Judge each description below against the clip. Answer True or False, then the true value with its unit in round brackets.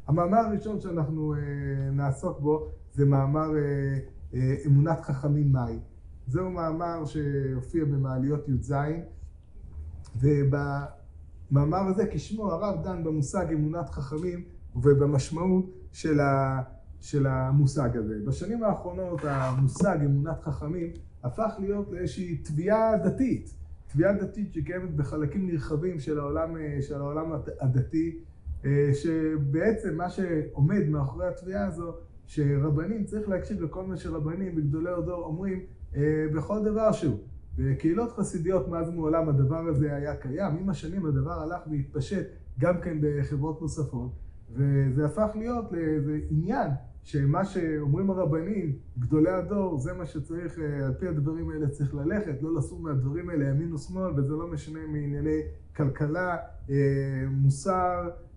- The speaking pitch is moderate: True (155 Hz)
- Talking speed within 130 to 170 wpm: False (115 wpm)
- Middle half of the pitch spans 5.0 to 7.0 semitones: False (4.0 semitones)